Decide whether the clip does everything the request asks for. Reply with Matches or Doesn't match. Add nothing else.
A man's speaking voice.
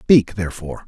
Matches